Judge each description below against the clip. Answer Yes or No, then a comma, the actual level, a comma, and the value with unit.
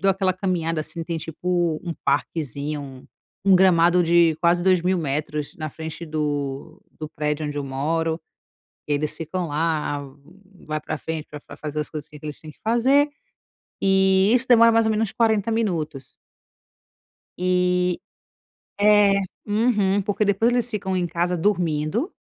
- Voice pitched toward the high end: No, medium, 170 Hz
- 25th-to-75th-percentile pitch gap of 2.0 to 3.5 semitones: No, average, 4.3 semitones